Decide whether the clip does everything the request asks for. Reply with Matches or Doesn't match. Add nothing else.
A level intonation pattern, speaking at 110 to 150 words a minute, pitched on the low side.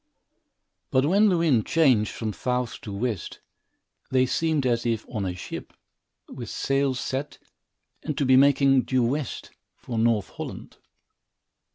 Doesn't match